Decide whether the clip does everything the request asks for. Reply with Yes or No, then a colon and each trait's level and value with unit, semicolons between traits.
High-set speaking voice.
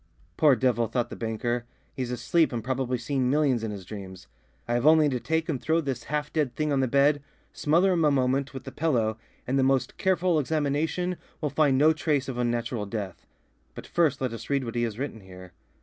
No: low, 130 Hz